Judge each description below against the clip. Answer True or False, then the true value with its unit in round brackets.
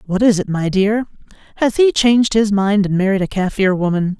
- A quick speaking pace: True (215 wpm)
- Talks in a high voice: True (205 Hz)